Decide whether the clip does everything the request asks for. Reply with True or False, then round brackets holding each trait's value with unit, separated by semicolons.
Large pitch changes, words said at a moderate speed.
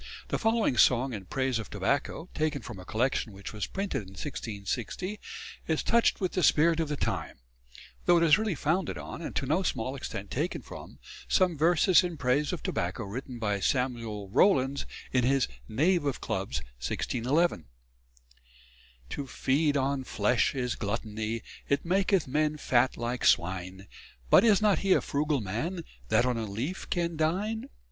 True (6.8 semitones; 170 wpm)